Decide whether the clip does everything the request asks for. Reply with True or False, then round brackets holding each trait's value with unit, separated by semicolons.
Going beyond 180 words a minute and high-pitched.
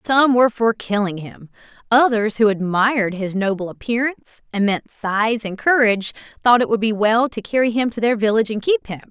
True (190 wpm; 220 Hz)